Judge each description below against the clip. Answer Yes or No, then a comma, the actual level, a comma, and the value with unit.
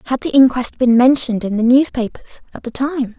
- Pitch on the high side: Yes, very high, 250 Hz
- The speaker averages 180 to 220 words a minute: Yes, fast, 205 wpm